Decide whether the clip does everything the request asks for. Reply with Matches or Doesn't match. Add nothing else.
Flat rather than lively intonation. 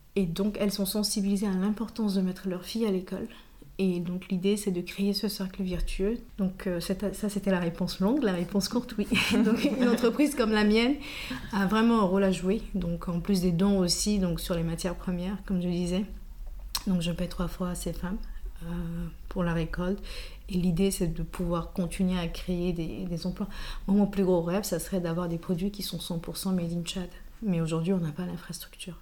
Matches